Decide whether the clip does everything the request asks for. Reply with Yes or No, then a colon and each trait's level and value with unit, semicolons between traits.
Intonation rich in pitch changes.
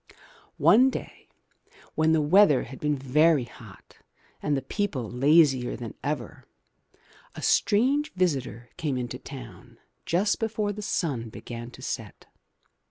Yes: wide, 6.7 semitones